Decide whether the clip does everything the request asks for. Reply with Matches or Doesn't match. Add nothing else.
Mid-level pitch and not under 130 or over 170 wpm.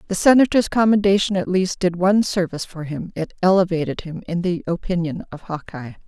Doesn't match